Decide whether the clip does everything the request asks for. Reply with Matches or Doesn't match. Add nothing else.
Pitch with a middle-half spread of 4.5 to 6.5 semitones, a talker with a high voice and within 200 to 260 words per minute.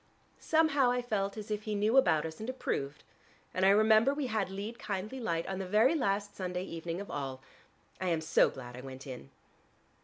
Matches